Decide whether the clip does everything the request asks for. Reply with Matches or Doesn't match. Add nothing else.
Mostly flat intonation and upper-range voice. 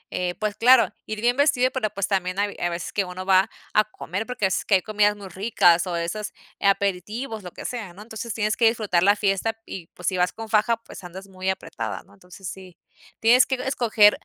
Doesn't match